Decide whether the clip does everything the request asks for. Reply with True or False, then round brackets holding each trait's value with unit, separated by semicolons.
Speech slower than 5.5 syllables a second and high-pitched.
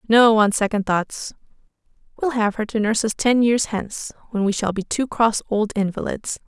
True (5.1 syllables/s; 220 Hz)